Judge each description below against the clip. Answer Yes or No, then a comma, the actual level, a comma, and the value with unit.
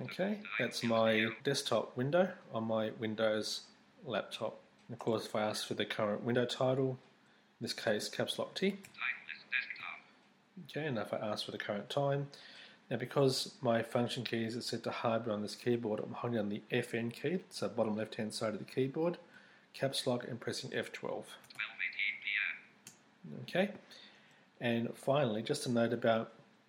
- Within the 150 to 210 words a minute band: Yes, average, 160 wpm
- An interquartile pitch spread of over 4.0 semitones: Yes, average, 4.5 semitones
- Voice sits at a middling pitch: No, low, 120 Hz